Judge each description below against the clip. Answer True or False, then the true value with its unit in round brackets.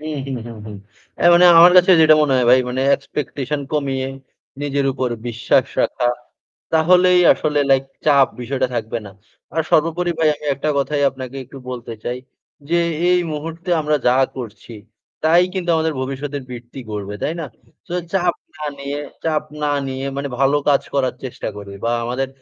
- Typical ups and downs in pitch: True (3.7 semitones)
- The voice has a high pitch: False (140 Hz)